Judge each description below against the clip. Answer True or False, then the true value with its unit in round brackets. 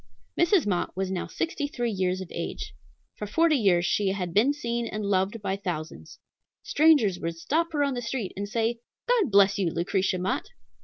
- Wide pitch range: True (6.1 semitones)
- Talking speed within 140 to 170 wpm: False (190 wpm)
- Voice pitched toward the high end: True (205 Hz)